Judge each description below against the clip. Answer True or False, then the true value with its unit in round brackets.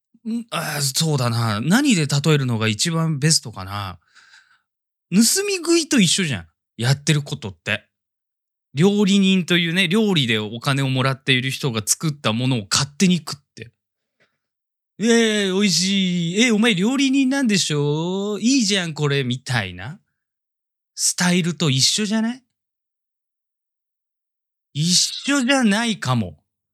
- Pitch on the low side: False (160 Hz)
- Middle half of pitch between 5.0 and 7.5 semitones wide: False (8.2 semitones)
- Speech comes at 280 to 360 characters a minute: False (270 characters per minute)